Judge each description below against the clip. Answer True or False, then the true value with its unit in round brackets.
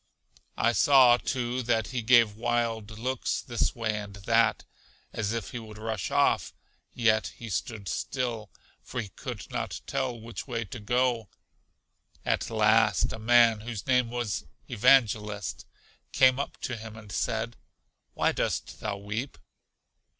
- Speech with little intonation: True (2.1 semitones)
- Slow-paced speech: False (145 wpm)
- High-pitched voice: False (115 Hz)